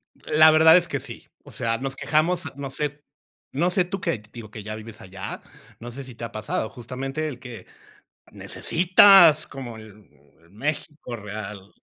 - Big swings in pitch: Yes, wide, 5.9 semitones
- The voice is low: Yes, low, 130 Hz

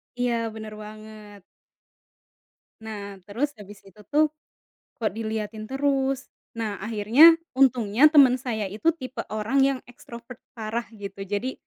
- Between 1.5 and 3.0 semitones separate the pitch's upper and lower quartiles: No, average, 3.7 semitones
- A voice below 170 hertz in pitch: No, high, 220 Hz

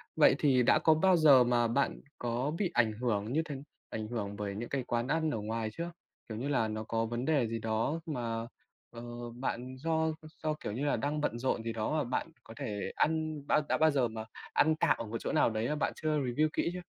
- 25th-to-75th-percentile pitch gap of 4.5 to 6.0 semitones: Yes, average, 5.1 semitones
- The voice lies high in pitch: No, low, 125 Hz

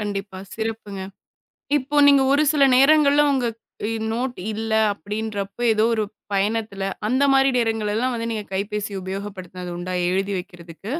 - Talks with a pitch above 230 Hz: No, high, 215 Hz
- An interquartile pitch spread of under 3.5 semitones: No, average, 3.9 semitones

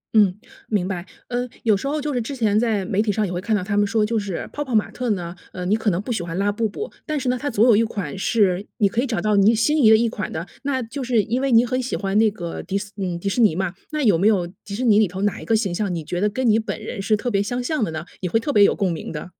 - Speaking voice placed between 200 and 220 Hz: Yes, high, 215 Hz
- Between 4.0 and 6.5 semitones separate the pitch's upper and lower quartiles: No, average, 3.6 semitones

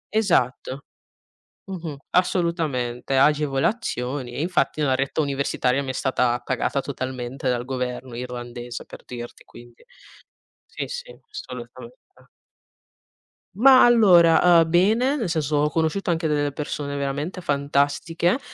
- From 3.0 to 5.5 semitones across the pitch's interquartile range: Yes, average, 5.0 semitones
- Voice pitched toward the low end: No, medium, 145 Hz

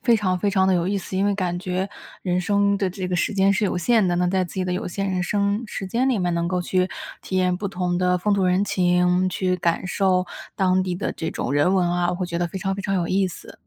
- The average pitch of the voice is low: No, medium, 185 Hz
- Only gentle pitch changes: Yes, narrow, 1.6 semitones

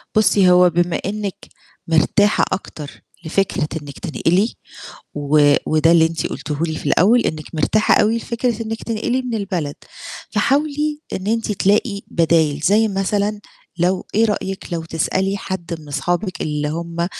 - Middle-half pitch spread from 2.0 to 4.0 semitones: No, average, 4.7 semitones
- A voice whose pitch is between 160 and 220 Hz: Yes, medium, 185 Hz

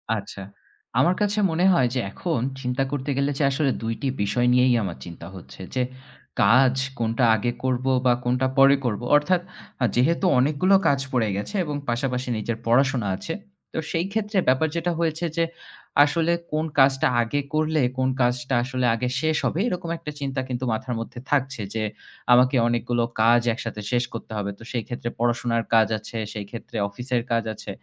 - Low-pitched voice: Yes, low, 130 Hz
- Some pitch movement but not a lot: Yes, average, 3.9 semitones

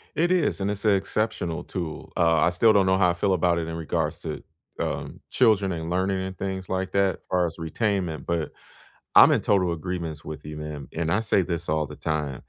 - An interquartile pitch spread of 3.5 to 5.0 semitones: No, average, 3.1 semitones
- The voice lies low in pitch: Yes, very low, 90 Hz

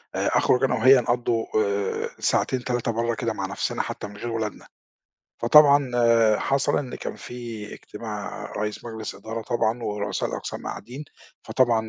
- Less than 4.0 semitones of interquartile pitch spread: Yes, narrow, 2.6 semitones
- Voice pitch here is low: Yes, low, 115 Hz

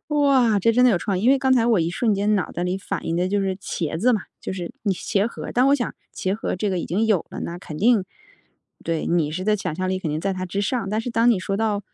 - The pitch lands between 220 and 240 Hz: No, high, 200 Hz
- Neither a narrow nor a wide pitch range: Yes, average, 3.8 semitones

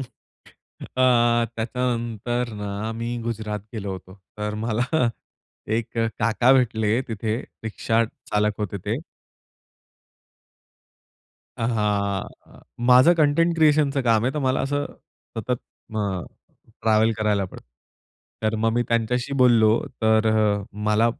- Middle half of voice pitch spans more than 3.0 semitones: No, average, 2.7 semitones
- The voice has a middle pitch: No, low, 115 Hz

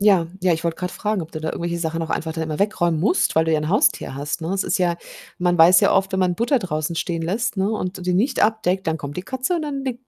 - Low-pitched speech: No, medium, 180 Hz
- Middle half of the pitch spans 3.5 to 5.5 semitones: Yes, average, 4.0 semitones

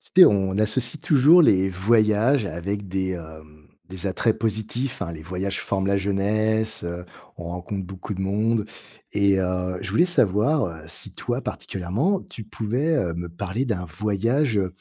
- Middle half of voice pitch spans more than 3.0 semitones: Yes, average, 3.5 semitones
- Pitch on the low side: Yes, low, 100 Hz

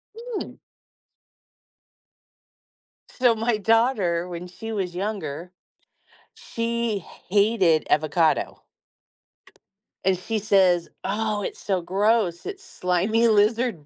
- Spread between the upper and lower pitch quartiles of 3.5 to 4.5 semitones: Yes, average, 4.2 semitones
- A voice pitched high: Yes, high, 205 Hz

